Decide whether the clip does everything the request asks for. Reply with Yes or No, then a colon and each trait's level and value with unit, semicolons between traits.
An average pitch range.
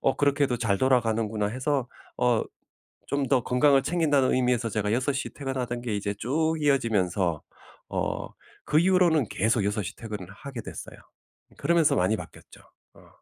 Yes: average, 4.5 semitones